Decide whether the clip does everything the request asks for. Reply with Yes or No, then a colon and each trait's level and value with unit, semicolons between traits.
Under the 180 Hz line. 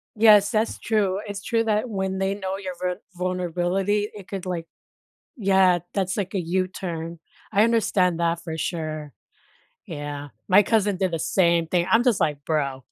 No: medium, 185 Hz